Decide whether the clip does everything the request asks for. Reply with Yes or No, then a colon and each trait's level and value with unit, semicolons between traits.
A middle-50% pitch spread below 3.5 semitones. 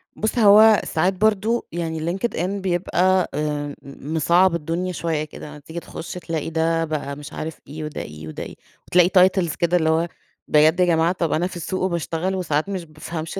Yes: average, 2.9 semitones